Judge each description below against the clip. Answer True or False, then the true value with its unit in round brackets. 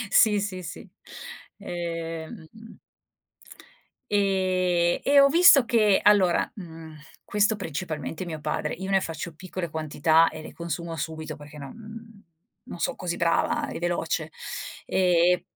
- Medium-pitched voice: True (175 Hz)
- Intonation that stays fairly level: False (3.9 semitones)